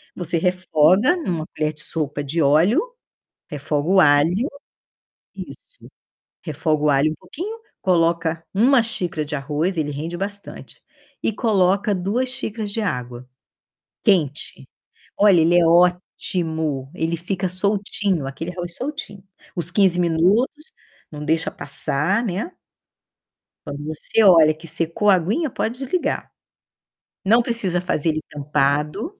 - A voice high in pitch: No, medium, 175 Hz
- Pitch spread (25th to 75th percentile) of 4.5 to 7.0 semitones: Yes, average, 4.8 semitones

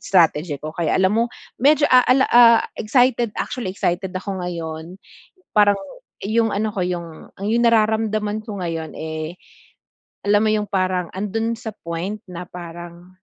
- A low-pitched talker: No, high, 200 Hz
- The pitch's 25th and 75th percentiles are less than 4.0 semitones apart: No, average, 4.3 semitones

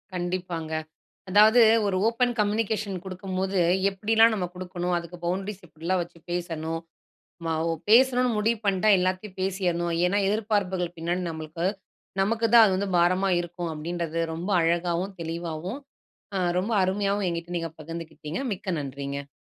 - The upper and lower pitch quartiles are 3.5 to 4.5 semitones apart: No, average, 3.1 semitones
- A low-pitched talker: No, medium, 185 Hz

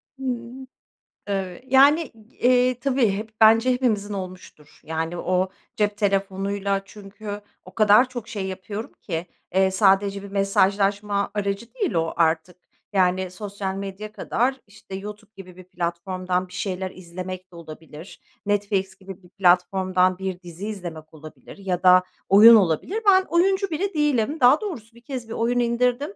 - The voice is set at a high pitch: Yes, high, 200 Hz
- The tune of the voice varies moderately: Yes, average, 4.0 semitones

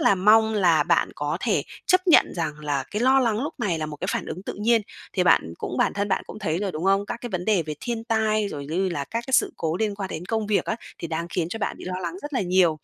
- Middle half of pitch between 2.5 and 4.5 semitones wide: No, average, 5.0 semitones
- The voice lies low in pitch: No, high, 195 Hz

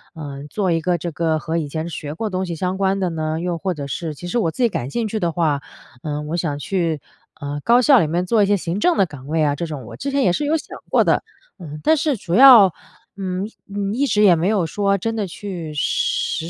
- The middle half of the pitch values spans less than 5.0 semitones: Yes, average, 4.6 semitones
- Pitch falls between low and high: Yes, medium, 175 Hz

